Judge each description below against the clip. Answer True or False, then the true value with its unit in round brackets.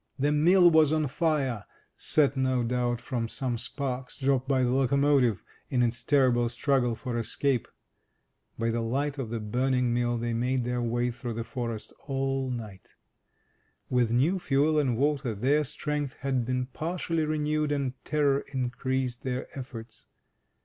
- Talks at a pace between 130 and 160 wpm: True (150 wpm)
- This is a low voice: True (130 Hz)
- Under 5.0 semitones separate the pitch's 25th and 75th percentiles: True (2.9 semitones)